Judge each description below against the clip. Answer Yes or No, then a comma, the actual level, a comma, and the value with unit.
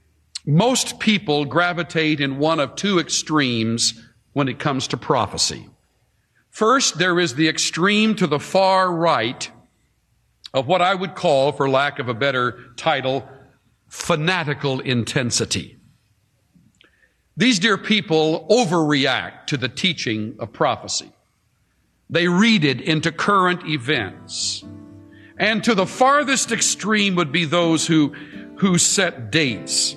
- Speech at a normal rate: No, slow, 125 wpm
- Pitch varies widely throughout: Yes, wide, 5.9 semitones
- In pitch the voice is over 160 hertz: No, medium, 155 Hz